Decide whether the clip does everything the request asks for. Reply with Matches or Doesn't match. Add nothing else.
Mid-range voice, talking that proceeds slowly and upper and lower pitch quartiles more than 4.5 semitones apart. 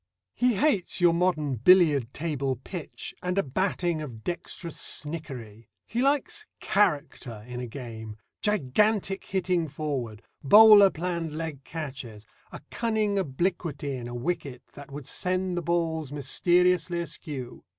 Matches